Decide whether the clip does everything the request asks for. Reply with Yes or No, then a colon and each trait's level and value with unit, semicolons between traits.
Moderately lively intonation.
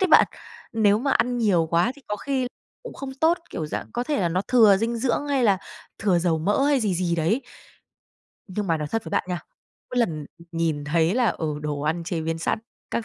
No: wide, 6.8 semitones